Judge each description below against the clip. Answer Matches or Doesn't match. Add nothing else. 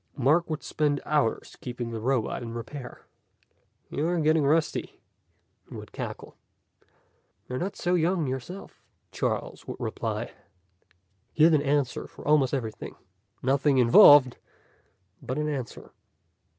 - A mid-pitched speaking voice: Matches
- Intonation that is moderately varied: Matches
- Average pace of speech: Doesn't match